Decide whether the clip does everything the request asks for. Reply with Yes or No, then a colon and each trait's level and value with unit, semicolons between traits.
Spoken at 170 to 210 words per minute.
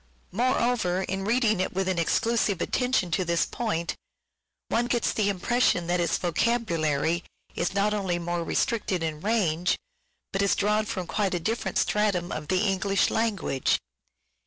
No: average, 155 wpm